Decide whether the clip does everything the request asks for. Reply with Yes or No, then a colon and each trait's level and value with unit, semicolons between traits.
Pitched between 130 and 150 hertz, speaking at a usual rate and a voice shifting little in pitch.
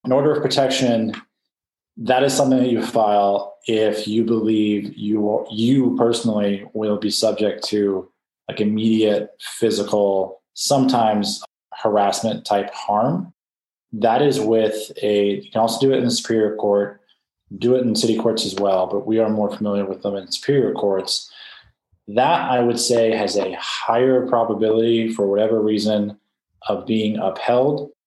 No: low, 110 Hz; average, 155 wpm; narrow, 2.3 semitones